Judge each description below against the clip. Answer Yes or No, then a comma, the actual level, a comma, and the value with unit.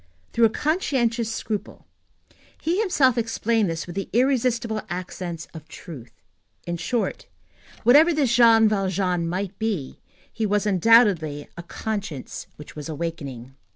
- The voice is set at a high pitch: Yes, high, 205 Hz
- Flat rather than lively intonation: No, wide, 5.6 semitones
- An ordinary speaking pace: No, slow, 130 wpm